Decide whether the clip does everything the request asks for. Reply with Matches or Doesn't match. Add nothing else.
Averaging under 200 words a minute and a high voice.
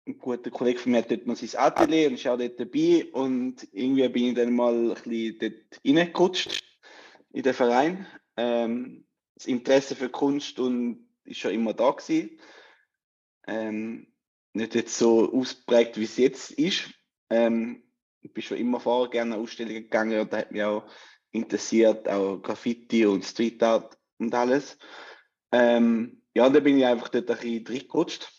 Doesn't match